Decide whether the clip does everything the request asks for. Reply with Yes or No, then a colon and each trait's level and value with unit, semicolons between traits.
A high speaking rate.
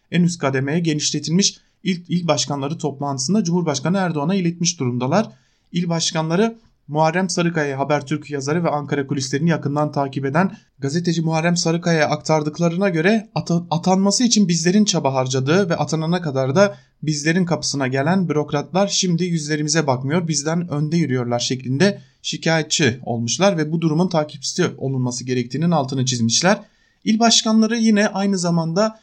No: average, 130 wpm